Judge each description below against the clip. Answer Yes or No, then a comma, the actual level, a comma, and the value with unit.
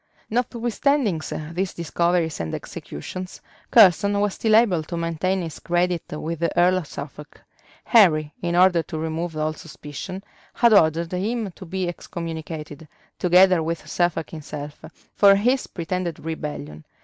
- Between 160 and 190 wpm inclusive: No, slow, 135 wpm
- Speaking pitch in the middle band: Yes, medium, 175 Hz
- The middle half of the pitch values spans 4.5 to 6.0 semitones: No, average, 3.2 semitones